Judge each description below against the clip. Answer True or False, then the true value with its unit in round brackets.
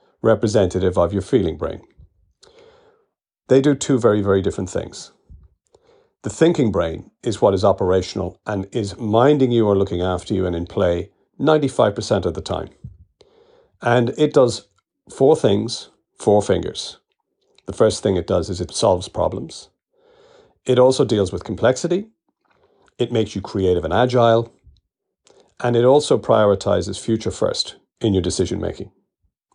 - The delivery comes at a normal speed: True (145 wpm)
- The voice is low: True (125 Hz)